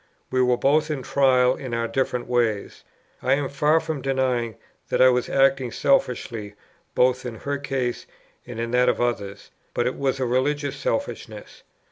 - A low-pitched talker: Yes, low, 125 Hz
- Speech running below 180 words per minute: Yes, average, 170 wpm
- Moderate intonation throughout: No, narrow, 2.1 semitones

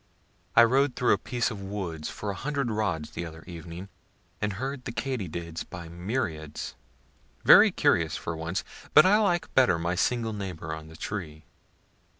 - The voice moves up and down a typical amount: No, wide, 6.3 semitones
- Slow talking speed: No, average, 165 wpm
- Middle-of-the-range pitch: No, very low, 95 Hz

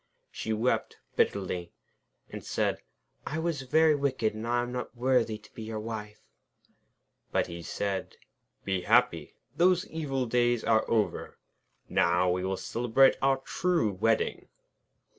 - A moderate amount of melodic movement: Yes, average, 4.2 semitones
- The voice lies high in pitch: No, low, 115 Hz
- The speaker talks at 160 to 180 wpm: No, average, 140 wpm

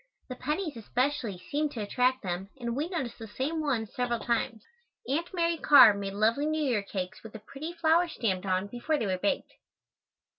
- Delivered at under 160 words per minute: No, average, 190 wpm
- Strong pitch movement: Yes, wide, 6.3 semitones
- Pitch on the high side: Yes, high, 245 Hz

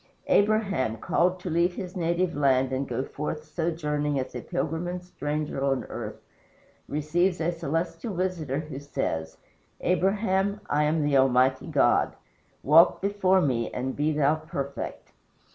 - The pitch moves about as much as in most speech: Yes, average, 4.4 semitones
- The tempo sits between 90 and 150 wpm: Yes, average, 145 wpm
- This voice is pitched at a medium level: Yes, medium, 155 Hz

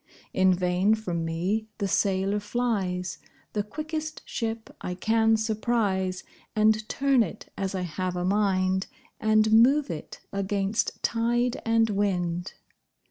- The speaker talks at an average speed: No, slow, 130 wpm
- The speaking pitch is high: Yes, high, 205 Hz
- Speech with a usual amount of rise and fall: Yes, average, 3.2 semitones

